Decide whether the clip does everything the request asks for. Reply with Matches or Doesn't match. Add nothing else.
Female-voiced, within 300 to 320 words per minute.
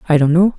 Matches